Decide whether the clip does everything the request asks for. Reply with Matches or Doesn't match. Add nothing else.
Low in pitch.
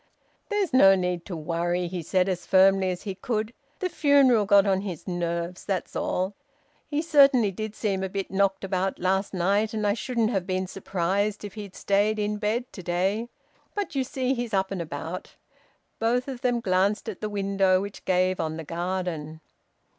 Doesn't match